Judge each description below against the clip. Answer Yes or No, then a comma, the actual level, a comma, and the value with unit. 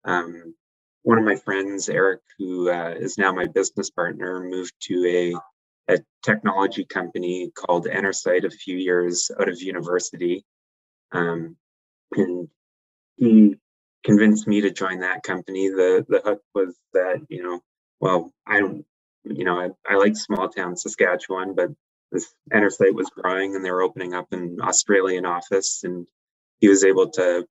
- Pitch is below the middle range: Yes, very low, 90 Hz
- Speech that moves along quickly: No, average, 155 wpm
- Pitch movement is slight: Yes, narrow, 1.8 semitones